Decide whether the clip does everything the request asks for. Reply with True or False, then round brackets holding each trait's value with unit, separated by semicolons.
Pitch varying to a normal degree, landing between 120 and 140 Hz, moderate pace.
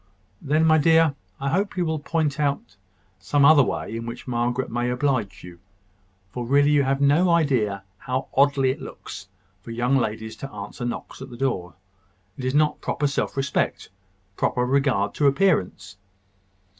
True (3.5 semitones; 135 Hz; 170 wpm)